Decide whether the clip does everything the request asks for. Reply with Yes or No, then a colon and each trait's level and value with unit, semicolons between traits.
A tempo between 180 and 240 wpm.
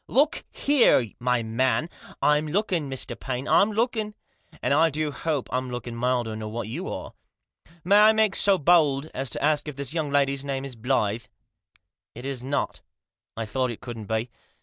Yes: average, 195 wpm